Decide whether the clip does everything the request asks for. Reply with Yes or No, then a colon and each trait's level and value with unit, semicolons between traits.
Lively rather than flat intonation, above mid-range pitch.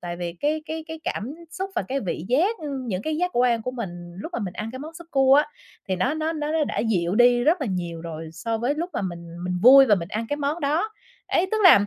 Yes: wide, 8.8 semitones; very high, 250 Hz